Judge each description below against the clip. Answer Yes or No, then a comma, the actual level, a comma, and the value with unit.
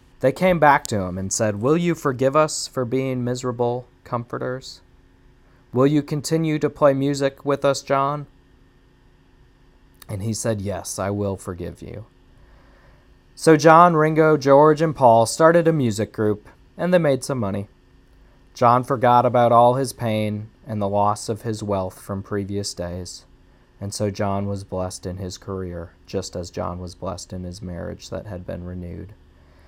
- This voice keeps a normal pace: Yes, average, 165 wpm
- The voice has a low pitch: Yes, low, 110 Hz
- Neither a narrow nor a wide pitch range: No, wide, 6.2 semitones